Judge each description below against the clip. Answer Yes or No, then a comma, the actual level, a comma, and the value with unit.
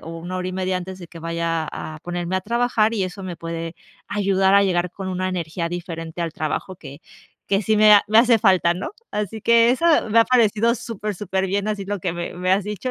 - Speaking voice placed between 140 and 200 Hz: Yes, medium, 185 Hz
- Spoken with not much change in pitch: No, average, 3.4 semitones